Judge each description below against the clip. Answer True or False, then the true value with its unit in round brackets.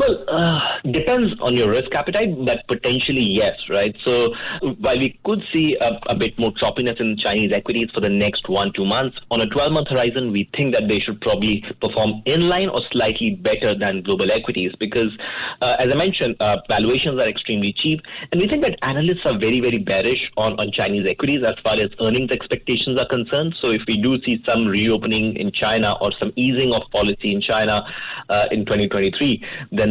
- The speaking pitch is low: True (120 Hz)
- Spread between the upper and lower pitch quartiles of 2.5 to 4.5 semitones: False (5.1 semitones)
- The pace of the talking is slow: False (200 wpm)